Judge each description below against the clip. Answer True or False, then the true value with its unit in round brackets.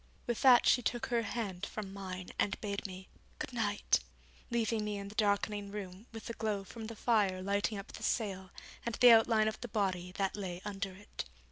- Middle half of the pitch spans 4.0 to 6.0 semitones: False (2.5 semitones)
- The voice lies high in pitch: True (205 Hz)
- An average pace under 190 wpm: False (205 wpm)